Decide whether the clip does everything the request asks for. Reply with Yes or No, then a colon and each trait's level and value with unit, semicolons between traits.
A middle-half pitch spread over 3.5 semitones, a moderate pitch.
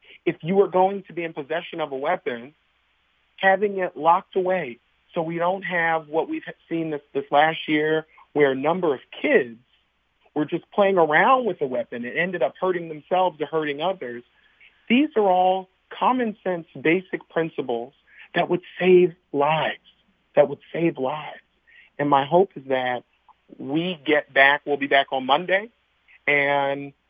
Yes: average, 4.2 semitones; medium, 160 Hz